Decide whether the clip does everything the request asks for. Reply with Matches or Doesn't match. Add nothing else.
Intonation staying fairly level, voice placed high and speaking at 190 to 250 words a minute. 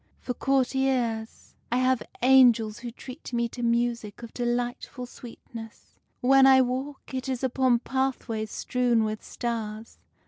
Doesn't match